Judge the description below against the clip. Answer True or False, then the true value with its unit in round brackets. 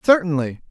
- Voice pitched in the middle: True (165 Hz)